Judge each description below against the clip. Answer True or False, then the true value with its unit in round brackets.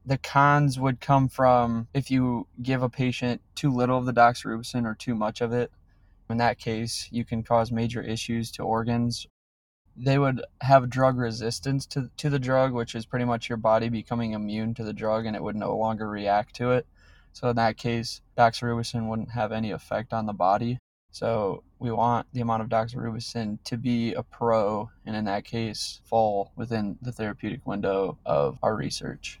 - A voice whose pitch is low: True (115 Hz)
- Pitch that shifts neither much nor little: False (2.1 semitones)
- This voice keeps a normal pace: True (190 wpm)